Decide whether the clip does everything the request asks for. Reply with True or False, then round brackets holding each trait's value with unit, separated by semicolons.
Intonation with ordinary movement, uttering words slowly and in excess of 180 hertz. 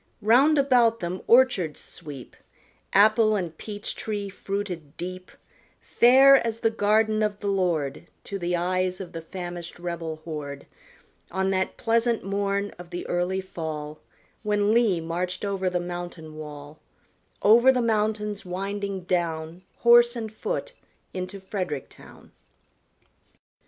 True (3.8 semitones; 130 wpm; 190 Hz)